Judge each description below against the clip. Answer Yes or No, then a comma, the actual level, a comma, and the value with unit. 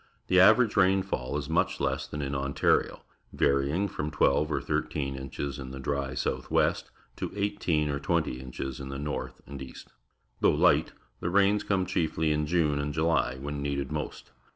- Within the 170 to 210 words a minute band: Yes, average, 175 wpm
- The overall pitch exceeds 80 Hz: No, very low, 75 Hz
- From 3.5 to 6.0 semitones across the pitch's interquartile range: Yes, average, 3.9 semitones